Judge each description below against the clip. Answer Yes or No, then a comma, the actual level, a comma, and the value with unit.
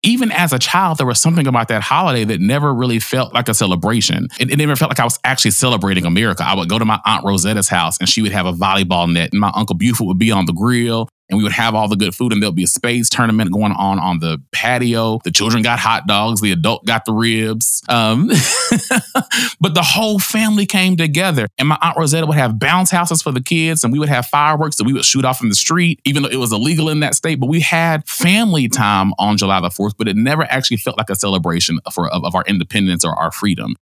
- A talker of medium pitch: No, low, 115 Hz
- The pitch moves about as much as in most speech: No, wide, 6.6 semitones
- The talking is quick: Yes, fast, 255 wpm